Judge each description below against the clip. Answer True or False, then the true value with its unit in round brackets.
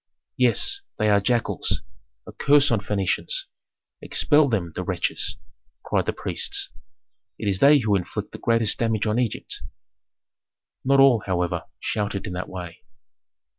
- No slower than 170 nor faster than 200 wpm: False (140 wpm)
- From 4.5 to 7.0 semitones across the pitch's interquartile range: True (5.0 semitones)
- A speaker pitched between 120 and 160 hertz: False (110 Hz)